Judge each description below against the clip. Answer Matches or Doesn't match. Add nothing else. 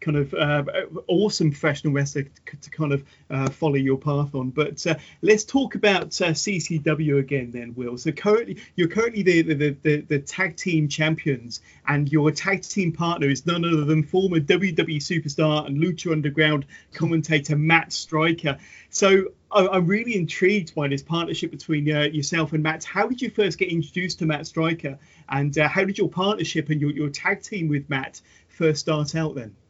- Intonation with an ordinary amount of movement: Matches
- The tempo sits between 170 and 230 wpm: Matches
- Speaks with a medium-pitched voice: Matches